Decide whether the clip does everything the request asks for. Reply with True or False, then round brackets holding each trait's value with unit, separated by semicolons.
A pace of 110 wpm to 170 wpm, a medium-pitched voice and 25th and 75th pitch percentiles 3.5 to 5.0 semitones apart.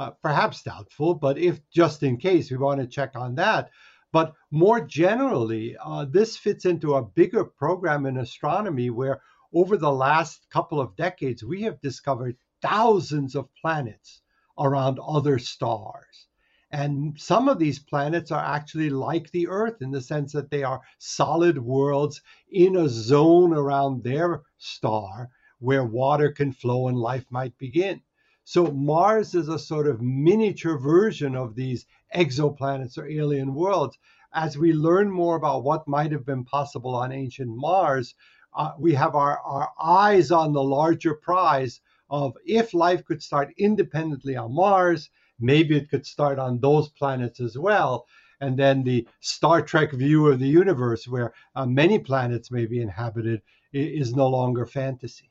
True (160 wpm; 145 Hz; 3.9 semitones)